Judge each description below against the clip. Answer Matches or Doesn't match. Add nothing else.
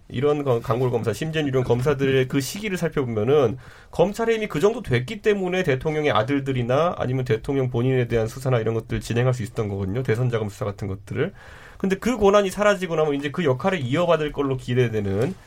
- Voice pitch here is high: Doesn't match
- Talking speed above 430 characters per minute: Matches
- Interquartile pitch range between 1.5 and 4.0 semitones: Doesn't match